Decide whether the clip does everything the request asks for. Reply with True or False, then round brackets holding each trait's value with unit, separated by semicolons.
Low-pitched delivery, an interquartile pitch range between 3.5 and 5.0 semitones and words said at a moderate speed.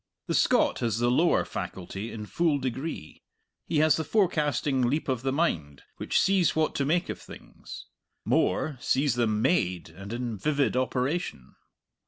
False (130 Hz; 5.5 semitones; 160 wpm)